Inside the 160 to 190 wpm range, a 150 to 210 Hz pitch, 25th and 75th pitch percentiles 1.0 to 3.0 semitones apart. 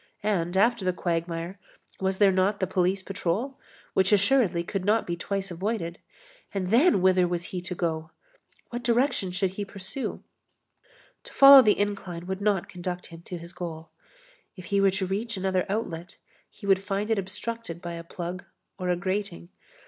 Yes: average, 175 wpm; high, 190 Hz; narrow, 2.6 semitones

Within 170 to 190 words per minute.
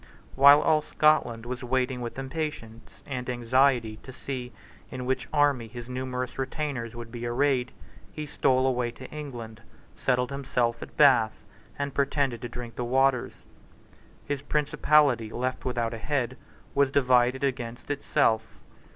No: average, 140 wpm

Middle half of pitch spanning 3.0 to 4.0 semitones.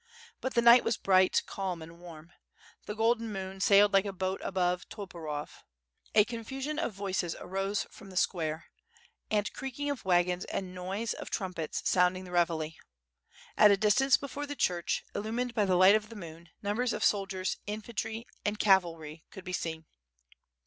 Yes: average, 3.5 semitones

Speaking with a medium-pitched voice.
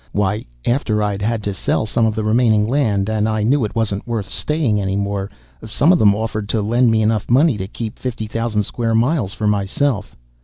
No: low, 110 Hz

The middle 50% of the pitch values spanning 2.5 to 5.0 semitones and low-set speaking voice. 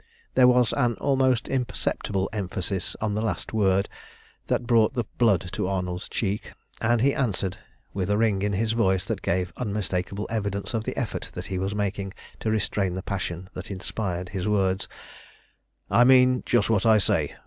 Yes: average, 3.3 semitones; low, 105 Hz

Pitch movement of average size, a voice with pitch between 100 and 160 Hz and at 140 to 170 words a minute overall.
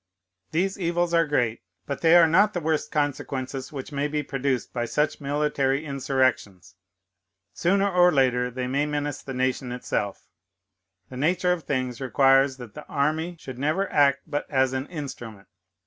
Yes: average, 3.3 semitones; medium, 140 Hz; average, 165 wpm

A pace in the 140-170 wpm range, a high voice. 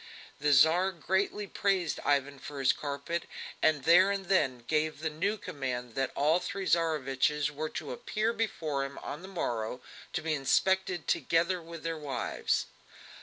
No: average, 160 wpm; medium, 155 Hz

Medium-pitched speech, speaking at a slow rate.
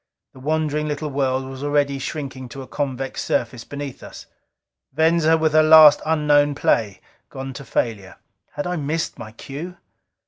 No: medium, 145 Hz; average, 160 wpm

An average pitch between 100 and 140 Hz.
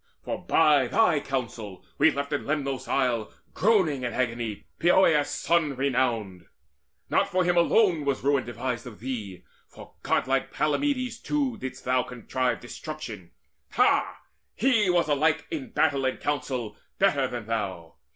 Yes: low, 135 Hz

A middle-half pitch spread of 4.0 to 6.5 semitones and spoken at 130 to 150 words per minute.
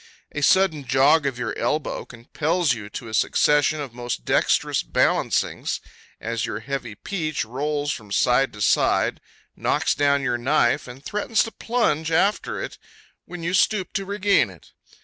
No: wide, 5.4 semitones; average, 160 wpm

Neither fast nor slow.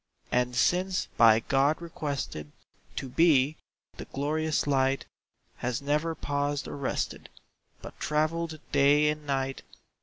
No: slow, 120 wpm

